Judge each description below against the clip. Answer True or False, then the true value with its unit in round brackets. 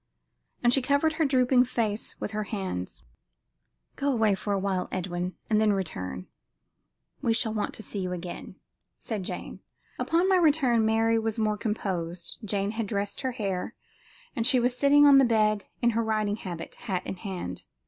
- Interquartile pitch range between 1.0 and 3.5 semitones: False (4.0 semitones)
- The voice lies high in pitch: True (215 Hz)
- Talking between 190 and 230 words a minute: False (175 wpm)